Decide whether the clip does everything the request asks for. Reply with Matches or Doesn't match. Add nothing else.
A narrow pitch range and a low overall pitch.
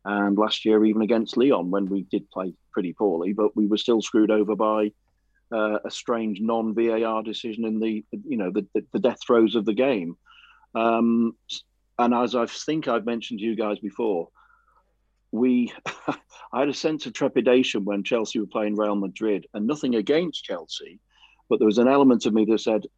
Matches